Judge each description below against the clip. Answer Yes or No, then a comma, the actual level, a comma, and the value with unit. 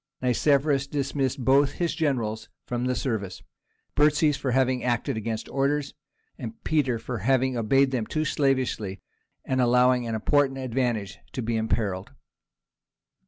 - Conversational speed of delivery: No, slow, 125 wpm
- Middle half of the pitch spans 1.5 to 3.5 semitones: Yes, average, 3.2 semitones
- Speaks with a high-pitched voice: No, low, 130 Hz